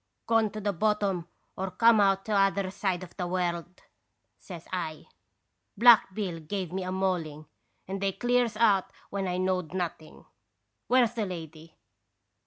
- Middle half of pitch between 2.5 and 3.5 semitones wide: Yes, average, 2.9 semitones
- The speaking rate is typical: Yes, average, 175 wpm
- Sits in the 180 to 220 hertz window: Yes, high, 190 Hz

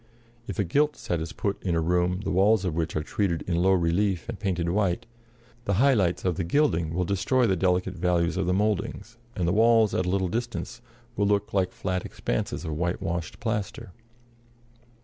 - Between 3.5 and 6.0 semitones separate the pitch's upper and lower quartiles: No, average, 3.1 semitones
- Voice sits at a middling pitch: No, very low, 95 Hz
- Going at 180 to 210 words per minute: Yes, average, 200 wpm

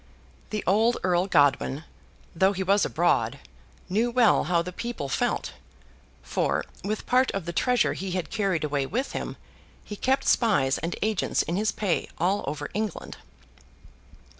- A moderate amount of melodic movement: Yes, average, 4.5 semitones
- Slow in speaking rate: No, average, 155 wpm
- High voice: Yes, high, 195 Hz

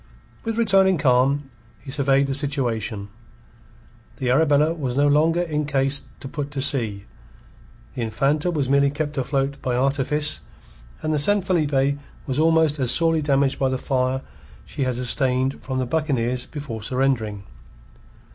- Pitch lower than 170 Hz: Yes, medium, 140 Hz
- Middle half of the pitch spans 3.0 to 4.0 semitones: No, narrow, 2.6 semitones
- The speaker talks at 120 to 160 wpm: Yes, average, 150 wpm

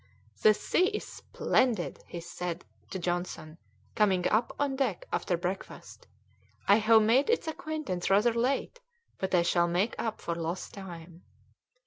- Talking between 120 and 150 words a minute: Yes, average, 145 wpm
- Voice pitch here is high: Yes, high, 195 Hz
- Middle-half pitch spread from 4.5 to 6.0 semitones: Yes, wide, 5.4 semitones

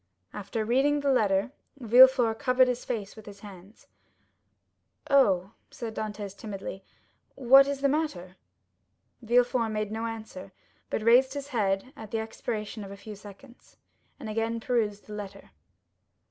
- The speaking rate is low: No, average, 145 wpm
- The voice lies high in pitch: Yes, high, 225 Hz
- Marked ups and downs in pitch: No, average, 3.6 semitones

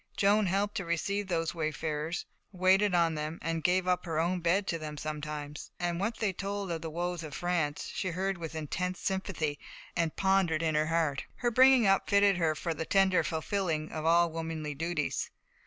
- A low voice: No, medium, 170 Hz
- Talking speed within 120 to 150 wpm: No, average, 190 wpm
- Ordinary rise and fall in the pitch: Yes, average, 3.4 semitones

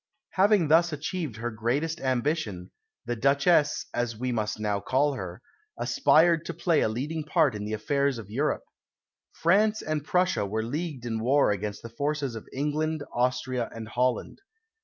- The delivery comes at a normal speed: Yes, average, 160 wpm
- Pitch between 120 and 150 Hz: Yes, low, 135 Hz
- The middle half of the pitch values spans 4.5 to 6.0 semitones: Yes, wide, 5.6 semitones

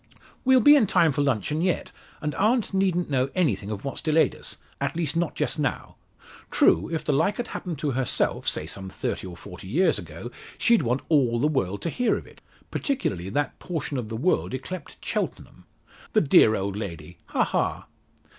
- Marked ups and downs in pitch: Yes, wide, 8.4 semitones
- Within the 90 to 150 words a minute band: No, average, 195 wpm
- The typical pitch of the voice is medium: Yes, medium, 145 Hz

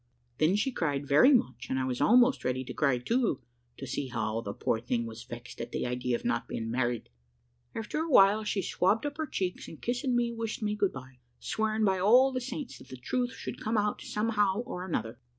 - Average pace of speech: No, fast, 220 wpm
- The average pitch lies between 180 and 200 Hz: Yes, high, 190 Hz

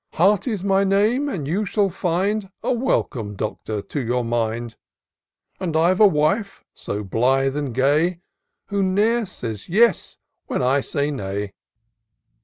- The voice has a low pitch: No, medium, 165 Hz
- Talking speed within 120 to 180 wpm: Yes, average, 140 wpm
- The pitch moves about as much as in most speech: No, wide, 8.2 semitones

